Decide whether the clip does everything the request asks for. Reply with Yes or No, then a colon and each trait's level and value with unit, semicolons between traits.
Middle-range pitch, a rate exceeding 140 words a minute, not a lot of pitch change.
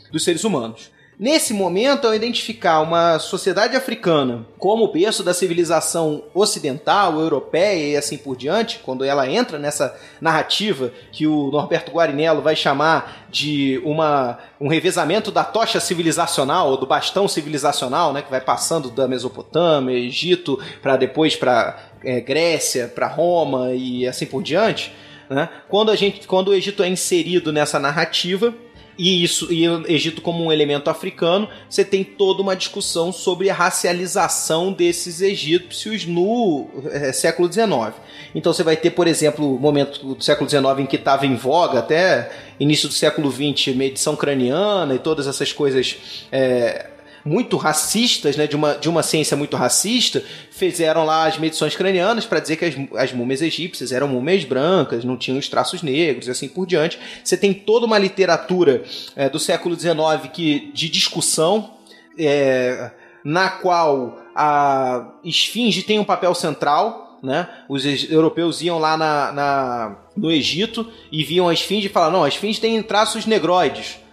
No: medium, 160 Hz; average, 160 wpm; average, 4.7 semitones